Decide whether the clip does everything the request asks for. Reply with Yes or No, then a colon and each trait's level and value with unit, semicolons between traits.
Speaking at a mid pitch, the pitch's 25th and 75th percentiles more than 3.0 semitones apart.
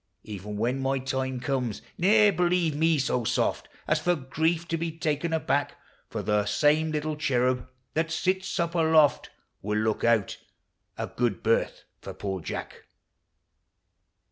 Yes: medium, 145 Hz; average, 5.1 semitones